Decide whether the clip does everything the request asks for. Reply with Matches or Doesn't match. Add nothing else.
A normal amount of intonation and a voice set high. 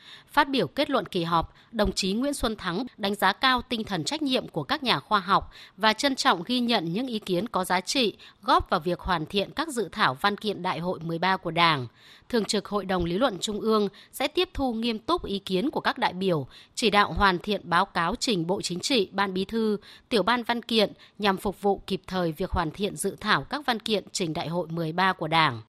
Matches